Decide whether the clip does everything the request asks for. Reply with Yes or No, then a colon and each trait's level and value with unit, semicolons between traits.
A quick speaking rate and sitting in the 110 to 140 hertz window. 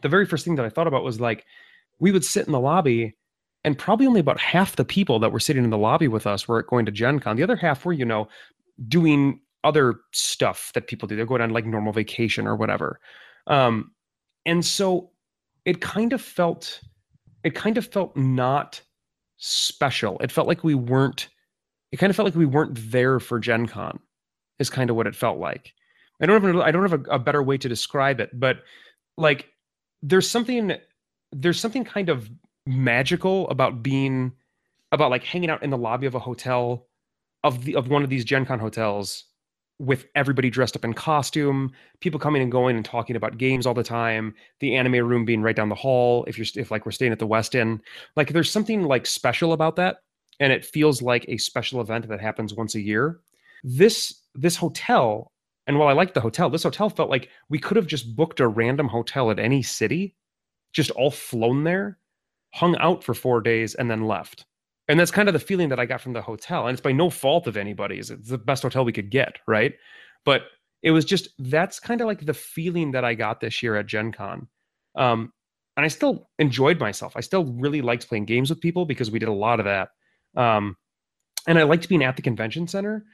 Yes: fast, 215 wpm; low, 135 Hz